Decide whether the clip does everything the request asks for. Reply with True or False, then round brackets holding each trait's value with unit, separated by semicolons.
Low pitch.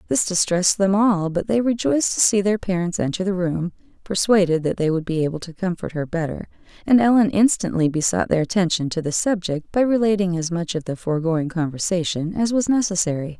False (180 Hz)